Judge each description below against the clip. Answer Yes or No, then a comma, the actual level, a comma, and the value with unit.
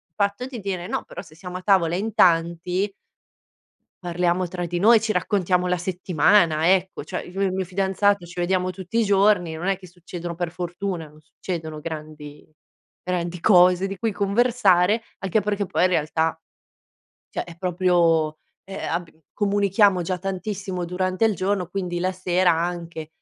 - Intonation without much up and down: Yes, narrow, 2.3 semitones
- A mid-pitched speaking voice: Yes, medium, 180 Hz